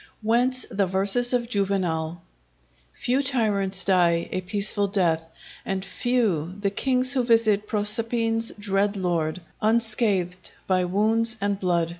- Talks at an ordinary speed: No, slow, 125 wpm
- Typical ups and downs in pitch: Yes, average, 3.7 semitones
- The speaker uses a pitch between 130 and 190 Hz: No, high, 200 Hz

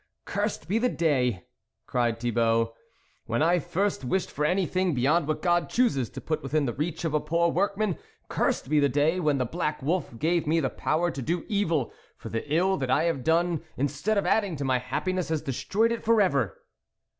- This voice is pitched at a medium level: Yes, medium, 160 Hz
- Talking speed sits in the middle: No, fast, 215 wpm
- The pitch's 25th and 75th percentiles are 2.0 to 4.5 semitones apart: No, average, 5.2 semitones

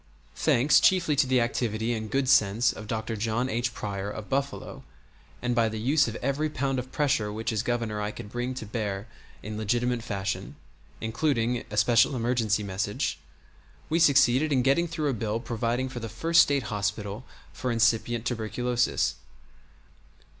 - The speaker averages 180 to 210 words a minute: No, average, 165 wpm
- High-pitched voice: No, low, 120 Hz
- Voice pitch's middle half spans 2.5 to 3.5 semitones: Yes, average, 3.2 semitones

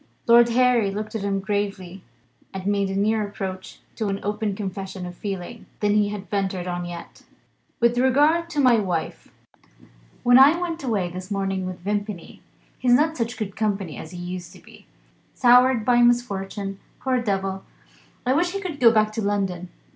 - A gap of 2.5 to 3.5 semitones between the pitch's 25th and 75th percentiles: No, average, 4.0 semitones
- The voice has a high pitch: Yes, high, 205 Hz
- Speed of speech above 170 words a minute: Yes, average, 180 wpm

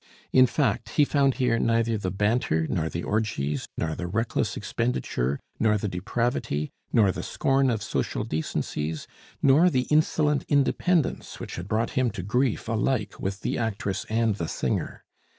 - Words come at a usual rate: Yes, average, 160 wpm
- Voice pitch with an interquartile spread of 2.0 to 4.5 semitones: No, wide, 5.5 semitones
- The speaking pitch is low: Yes, low, 110 Hz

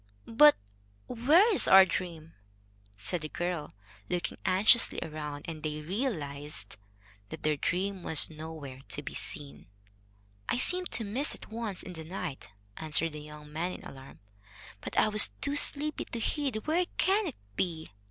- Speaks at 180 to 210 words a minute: No, average, 160 wpm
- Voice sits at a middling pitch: Yes, medium, 175 Hz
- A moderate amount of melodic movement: No, wide, 7.4 semitones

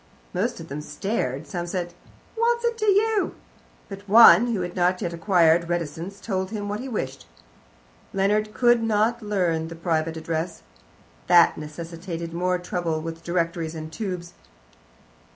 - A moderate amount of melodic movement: Yes, average, 4.1 semitones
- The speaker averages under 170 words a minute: Yes, average, 150 wpm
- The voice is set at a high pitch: No, medium, 180 Hz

